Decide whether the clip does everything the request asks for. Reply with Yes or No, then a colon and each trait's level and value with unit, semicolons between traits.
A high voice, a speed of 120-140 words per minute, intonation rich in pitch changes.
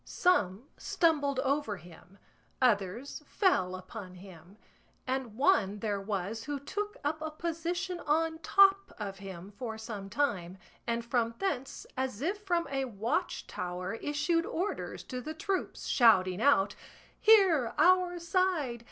Yes: very high, 260 Hz; slow, 135 wpm; wide, 8.6 semitones